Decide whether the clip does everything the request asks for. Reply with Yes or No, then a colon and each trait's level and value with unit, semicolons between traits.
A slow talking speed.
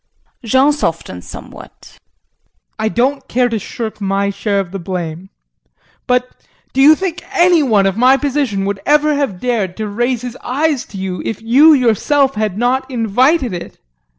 No: average, 165 wpm